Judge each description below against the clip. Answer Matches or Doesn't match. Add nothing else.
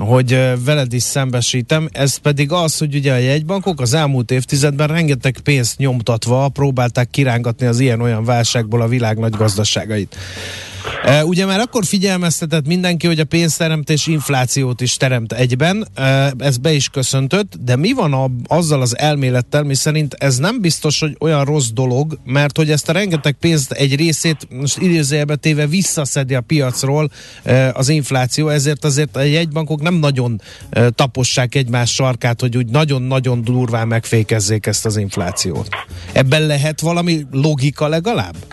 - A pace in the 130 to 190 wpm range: Matches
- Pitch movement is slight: Doesn't match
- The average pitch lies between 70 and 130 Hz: Doesn't match